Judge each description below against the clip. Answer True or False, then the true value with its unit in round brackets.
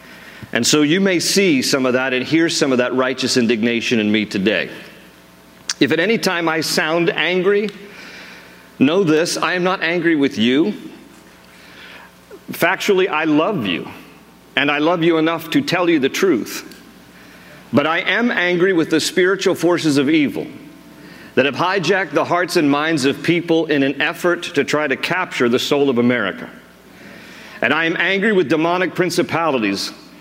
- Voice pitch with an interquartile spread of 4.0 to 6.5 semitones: True (5.1 semitones)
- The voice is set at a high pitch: False (160 Hz)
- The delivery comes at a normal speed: True (165 wpm)